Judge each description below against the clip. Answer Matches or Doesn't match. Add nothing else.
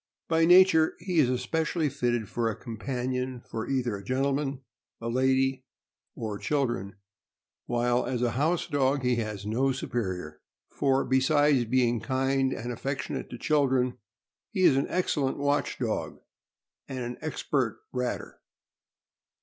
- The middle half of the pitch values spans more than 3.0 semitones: Doesn't match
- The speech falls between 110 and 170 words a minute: Matches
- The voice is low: Matches